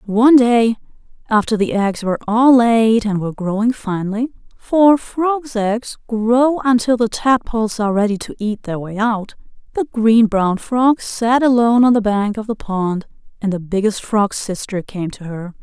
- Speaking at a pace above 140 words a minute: Yes, average, 175 wpm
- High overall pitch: Yes, high, 220 Hz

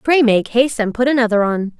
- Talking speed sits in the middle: No, fast, 235 wpm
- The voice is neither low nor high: No, high, 235 Hz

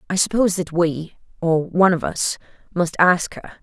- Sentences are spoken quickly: No, average, 150 wpm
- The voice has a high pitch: No, medium, 175 Hz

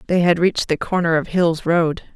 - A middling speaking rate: No, fast, 220 wpm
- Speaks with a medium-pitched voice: Yes, medium, 170 Hz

